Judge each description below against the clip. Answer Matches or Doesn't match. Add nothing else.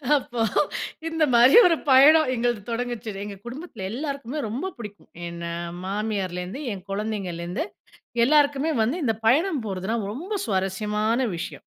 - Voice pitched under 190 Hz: Doesn't match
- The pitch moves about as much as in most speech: Doesn't match